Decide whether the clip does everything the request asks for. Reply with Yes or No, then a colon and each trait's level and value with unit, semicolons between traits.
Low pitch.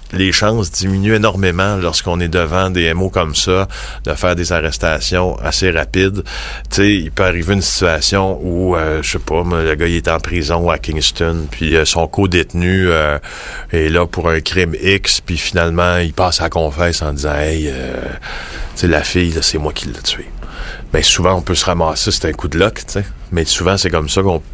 Yes: very low, 85 Hz